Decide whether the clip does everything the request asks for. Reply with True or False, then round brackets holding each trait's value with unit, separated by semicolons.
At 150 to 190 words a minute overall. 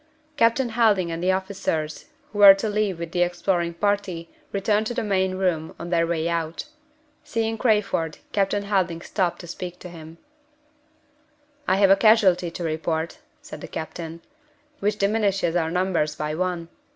True (165 wpm)